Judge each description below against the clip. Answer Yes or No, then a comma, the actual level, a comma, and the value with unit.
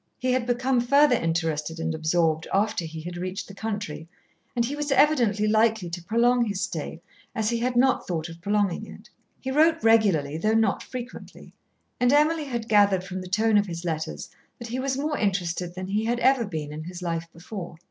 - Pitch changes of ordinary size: No, wide, 6.0 semitones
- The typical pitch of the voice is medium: No, high, 205 Hz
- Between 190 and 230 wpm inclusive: Yes, average, 200 wpm